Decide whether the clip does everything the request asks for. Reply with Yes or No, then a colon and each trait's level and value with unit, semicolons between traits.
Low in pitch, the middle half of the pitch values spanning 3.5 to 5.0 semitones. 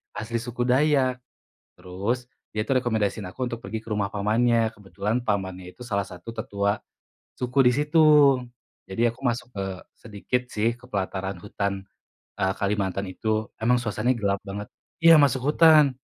Yes: low, 110 Hz; average, 3.8 semitones